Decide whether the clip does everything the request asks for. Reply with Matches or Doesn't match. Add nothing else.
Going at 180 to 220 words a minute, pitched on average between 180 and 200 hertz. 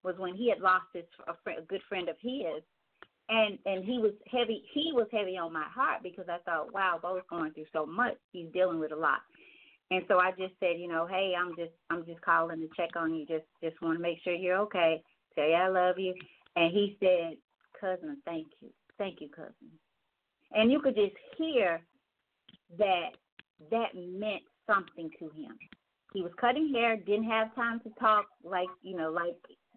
Matches